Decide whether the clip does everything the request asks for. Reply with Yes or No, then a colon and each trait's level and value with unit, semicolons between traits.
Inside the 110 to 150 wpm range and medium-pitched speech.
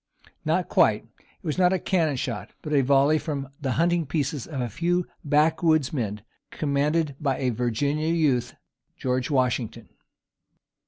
Yes: average, 145 wpm; medium, 145 Hz